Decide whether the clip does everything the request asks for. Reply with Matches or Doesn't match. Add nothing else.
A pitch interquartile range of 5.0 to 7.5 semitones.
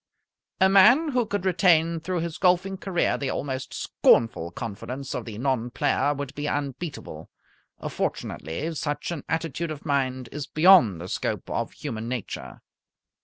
Matches